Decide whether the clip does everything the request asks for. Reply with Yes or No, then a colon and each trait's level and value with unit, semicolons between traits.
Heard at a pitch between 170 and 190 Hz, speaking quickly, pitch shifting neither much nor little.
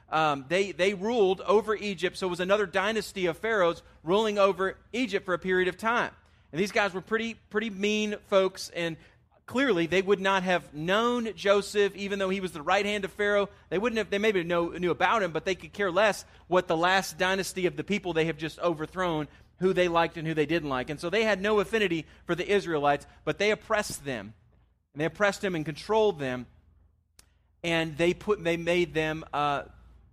Yes: medium, 185 Hz; fast, 210 wpm; average, 4.2 semitones